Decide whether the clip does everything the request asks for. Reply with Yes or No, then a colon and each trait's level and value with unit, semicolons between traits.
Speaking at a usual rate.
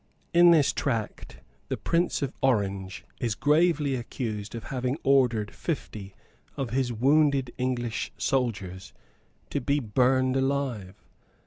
No: slow, 120 wpm